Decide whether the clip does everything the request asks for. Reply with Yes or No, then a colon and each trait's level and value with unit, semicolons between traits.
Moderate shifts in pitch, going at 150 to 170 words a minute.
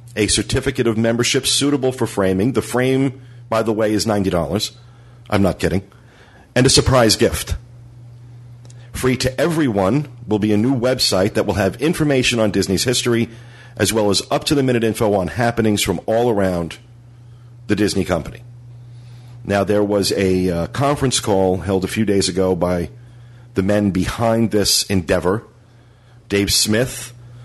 Yes: average, 3.1 semitones; average, 155 wpm